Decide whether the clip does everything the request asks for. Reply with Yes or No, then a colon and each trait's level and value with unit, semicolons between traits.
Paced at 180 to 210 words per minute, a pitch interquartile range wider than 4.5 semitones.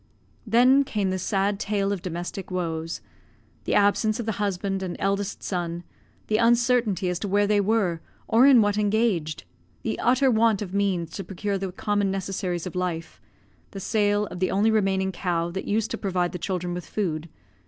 No: average, 185 wpm; average, 2.9 semitones